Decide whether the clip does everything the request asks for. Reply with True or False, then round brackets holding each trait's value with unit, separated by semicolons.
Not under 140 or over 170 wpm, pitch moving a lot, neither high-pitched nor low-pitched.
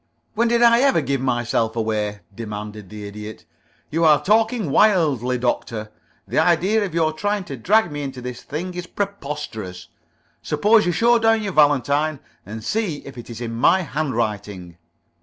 True (165 wpm; 8.8 semitones; 145 Hz)